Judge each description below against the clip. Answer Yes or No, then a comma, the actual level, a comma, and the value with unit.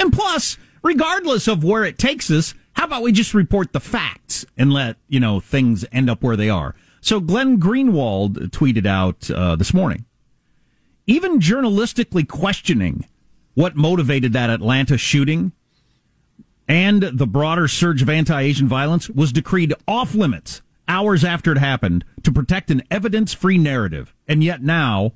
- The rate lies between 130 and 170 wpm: Yes, average, 155 wpm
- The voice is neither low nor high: Yes, medium, 150 Hz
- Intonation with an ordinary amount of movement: No, wide, 7.5 semitones